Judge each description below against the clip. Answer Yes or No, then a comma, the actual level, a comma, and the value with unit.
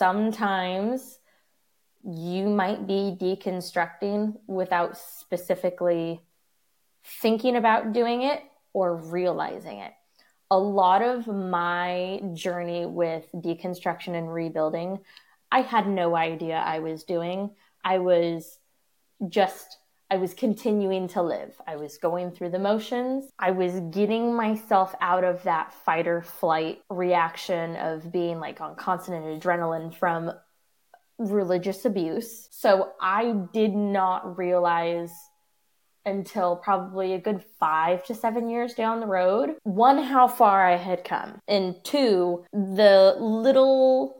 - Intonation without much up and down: No, average, 3.9 semitones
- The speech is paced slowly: Yes, slow, 120 wpm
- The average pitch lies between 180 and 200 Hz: Yes, medium, 185 Hz